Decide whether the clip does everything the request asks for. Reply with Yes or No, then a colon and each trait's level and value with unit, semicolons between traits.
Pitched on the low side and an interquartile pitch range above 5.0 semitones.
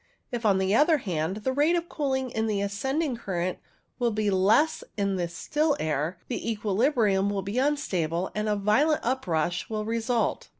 No: high, 215 Hz; wide, 5.6 semitones